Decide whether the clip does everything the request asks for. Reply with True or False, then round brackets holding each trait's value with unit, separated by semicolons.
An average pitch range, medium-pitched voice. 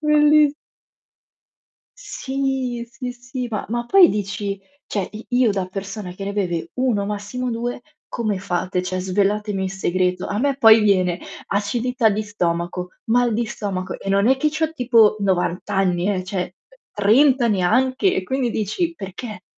False (4.5 semitones; 210 Hz)